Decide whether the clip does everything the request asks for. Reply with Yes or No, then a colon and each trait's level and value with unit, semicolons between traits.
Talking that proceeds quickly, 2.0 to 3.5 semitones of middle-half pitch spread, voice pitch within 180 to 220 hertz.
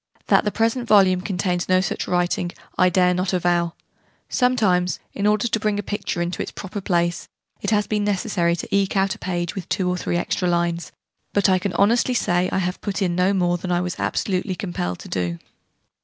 Yes: fast, 210 wpm; narrow, 2.5 semitones; medium, 185 Hz